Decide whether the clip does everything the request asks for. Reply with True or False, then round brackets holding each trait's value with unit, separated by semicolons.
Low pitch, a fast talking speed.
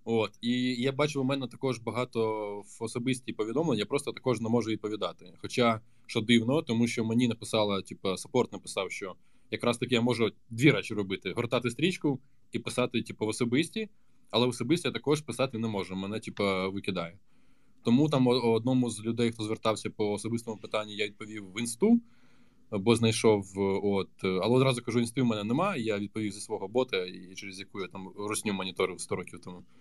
True (115 Hz; 185 wpm)